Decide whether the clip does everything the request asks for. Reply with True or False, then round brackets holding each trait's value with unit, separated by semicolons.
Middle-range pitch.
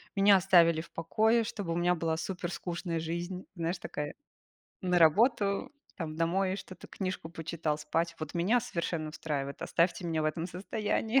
True (170 Hz)